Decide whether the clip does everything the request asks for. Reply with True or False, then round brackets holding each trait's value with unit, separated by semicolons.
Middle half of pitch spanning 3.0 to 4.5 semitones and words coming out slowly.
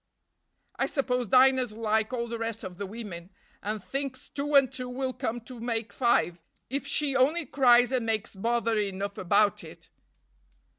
False (3.5 semitones; 165 wpm)